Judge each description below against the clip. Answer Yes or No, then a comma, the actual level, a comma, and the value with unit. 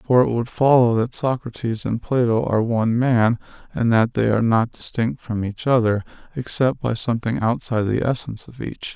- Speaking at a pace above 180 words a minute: Yes, average, 190 wpm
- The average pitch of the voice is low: Yes, low, 115 Hz